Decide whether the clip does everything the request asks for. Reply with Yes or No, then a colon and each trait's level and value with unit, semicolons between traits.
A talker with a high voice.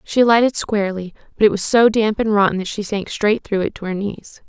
Yes: high, 210 Hz